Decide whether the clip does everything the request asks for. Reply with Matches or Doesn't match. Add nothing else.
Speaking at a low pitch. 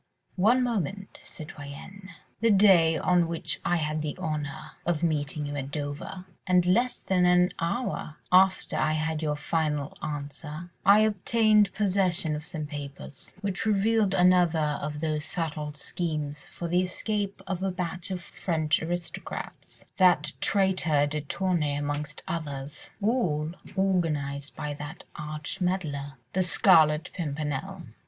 Doesn't match